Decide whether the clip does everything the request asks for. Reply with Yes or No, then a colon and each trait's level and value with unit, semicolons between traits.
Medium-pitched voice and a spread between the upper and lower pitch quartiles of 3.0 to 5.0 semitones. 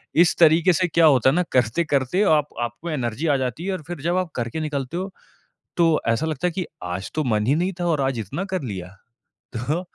No: medium, 155 Hz; wide, 5.4 semitones